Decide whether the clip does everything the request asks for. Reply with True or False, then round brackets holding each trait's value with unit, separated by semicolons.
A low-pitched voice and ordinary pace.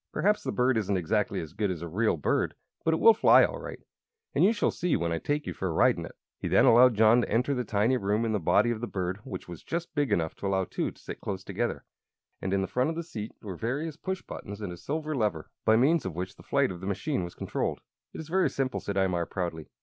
False (110 Hz; 270 wpm)